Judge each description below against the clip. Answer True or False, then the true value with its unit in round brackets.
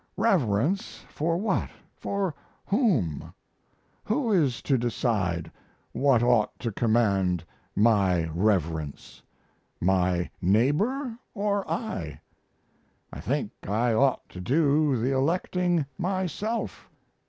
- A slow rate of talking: True (95 wpm)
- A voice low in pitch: True (130 Hz)